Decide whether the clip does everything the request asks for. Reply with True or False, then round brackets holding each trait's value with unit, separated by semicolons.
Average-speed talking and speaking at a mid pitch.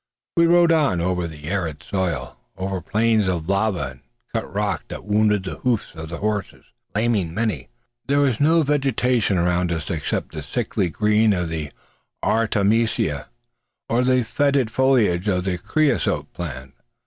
False (155 wpm; 105 Hz)